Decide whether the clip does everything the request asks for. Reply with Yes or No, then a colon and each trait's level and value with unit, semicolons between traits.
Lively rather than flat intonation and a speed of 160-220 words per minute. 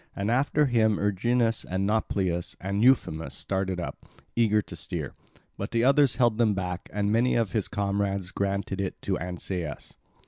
No: average, 3.5 semitones; average, 165 wpm